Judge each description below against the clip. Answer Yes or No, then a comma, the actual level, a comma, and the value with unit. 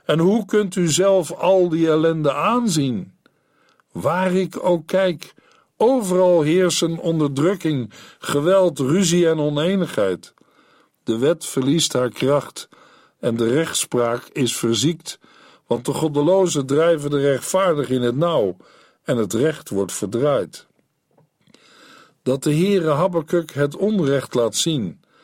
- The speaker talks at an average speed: No, slow, 125 wpm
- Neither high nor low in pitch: Yes, medium, 160 Hz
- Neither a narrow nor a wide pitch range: Yes, average, 4.8 semitones